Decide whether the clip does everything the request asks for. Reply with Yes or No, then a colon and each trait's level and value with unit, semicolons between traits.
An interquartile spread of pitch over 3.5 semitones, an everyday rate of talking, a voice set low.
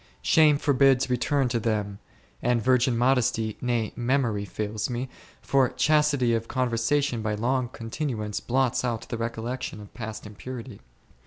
No: average, 2.7 semitones; average, 150 wpm; low, 120 Hz